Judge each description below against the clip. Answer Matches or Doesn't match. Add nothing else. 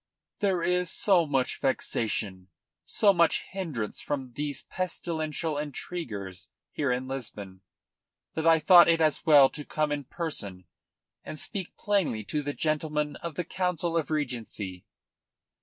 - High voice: Doesn't match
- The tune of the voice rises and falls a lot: Doesn't match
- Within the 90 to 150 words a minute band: Matches